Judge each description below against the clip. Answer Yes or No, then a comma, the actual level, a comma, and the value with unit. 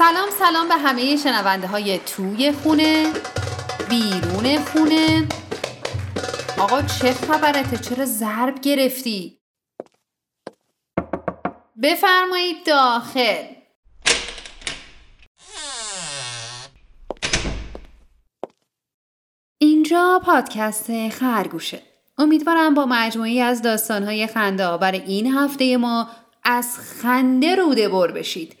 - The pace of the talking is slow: Yes, slow, 75 wpm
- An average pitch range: No, wide, 6.4 semitones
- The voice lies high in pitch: Yes, very high, 250 Hz